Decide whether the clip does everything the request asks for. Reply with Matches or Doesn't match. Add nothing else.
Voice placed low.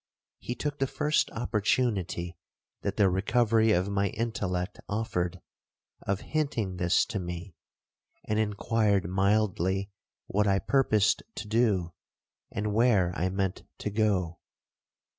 Matches